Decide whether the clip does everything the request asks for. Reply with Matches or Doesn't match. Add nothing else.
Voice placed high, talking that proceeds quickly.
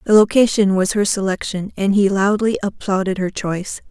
Doesn't match